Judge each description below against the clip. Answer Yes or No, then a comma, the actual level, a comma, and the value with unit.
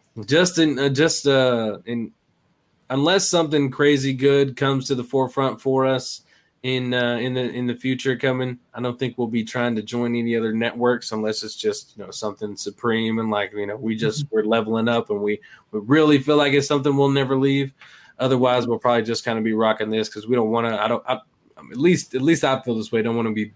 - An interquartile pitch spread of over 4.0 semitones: No, average, 3.5 semitones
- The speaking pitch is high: No, low, 125 Hz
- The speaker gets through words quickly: Yes, fast, 235 wpm